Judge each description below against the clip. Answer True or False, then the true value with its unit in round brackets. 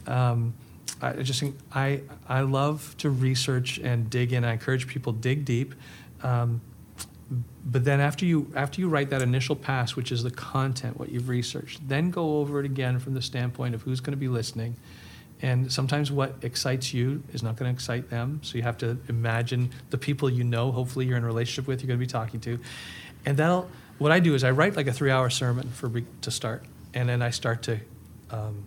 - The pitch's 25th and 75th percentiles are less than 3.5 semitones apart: True (2.5 semitones)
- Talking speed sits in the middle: False (220 wpm)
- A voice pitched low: True (125 Hz)